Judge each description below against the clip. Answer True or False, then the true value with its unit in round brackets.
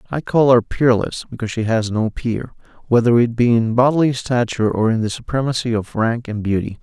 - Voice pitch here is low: True (120 Hz)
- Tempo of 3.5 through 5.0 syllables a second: False (5.7 syllables/s)